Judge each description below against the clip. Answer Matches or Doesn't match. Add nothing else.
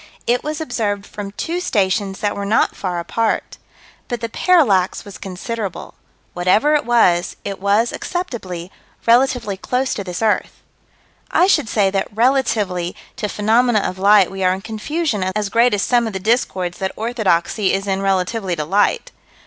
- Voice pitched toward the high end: Matches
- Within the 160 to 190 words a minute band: Matches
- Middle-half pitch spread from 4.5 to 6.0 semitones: Doesn't match